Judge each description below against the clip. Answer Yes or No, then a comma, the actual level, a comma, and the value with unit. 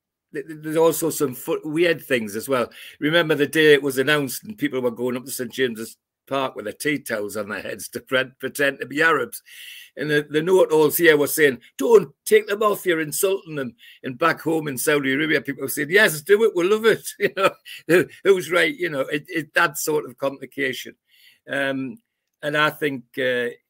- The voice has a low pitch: No, medium, 150 Hz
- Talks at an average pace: No, fast, 210 wpm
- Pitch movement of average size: Yes, average, 4.3 semitones